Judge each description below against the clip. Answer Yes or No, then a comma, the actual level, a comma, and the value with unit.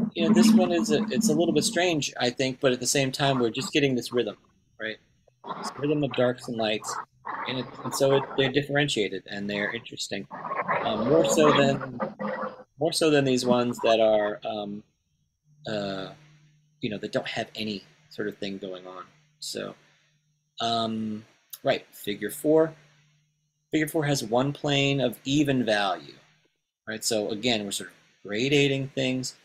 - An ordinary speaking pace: Yes, average, 170 wpm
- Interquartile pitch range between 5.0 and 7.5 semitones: Yes, average, 5.3 semitones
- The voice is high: No, low, 135 Hz